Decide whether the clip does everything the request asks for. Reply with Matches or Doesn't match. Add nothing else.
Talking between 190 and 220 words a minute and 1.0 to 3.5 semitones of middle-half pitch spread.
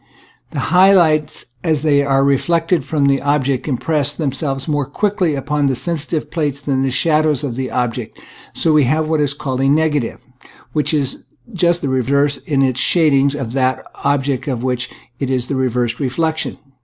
Matches